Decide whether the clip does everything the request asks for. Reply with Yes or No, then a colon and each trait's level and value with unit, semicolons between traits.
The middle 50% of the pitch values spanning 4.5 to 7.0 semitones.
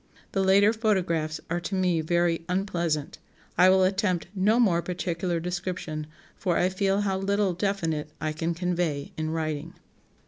No: average, 2.8 semitones